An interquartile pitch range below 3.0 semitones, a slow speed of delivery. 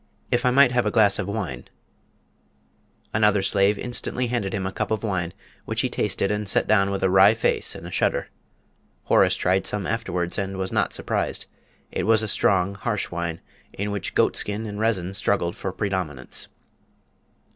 No: narrow, 2.4 semitones; average, 180 wpm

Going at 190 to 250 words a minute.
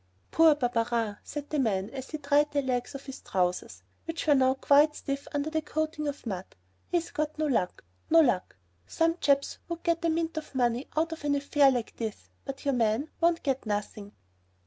Yes: average, 200 wpm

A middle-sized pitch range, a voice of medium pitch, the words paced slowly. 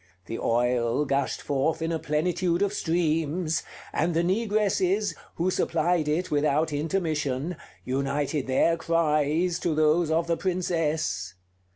Yes: average, 3.0 semitones; medium, 160 Hz; slow, 130 wpm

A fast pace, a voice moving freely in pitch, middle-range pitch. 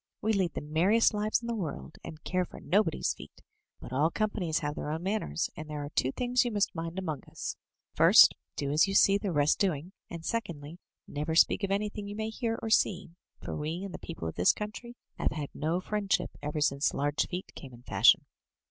Yes: fast, 220 wpm; wide, 5.7 semitones; medium, 175 Hz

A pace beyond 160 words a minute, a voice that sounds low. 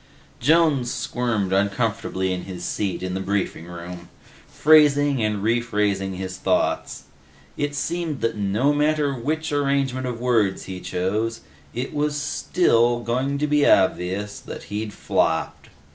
No: slow, 135 wpm; low, 115 Hz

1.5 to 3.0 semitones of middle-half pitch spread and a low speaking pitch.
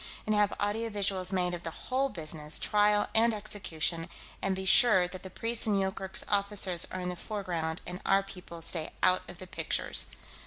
No: average, 2.7 semitones; high, 190 Hz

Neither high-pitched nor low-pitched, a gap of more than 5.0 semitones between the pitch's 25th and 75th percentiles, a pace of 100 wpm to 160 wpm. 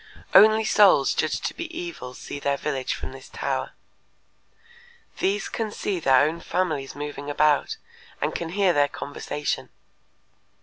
Yes: medium, 155 Hz; wide, 5.6 semitones; average, 140 wpm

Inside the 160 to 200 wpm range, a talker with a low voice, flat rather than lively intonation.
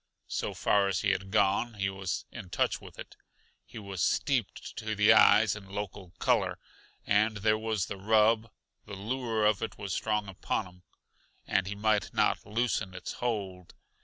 Yes: average, 175 wpm; low, 105 Hz; narrow, 2.1 semitones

